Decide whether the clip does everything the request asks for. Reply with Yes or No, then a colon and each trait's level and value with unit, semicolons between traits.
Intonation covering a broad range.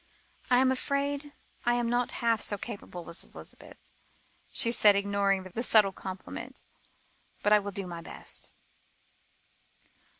No: average, 3.7 semitones